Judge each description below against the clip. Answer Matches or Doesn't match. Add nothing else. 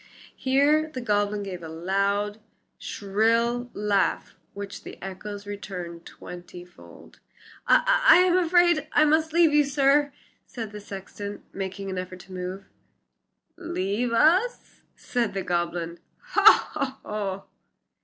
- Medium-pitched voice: Doesn't match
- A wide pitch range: Matches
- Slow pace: Matches